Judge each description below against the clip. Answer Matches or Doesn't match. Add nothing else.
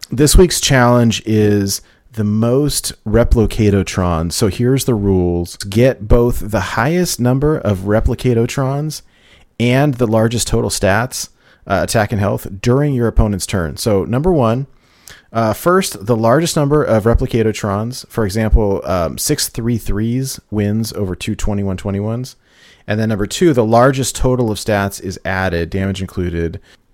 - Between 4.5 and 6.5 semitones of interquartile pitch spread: Doesn't match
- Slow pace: Doesn't match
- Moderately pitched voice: Doesn't match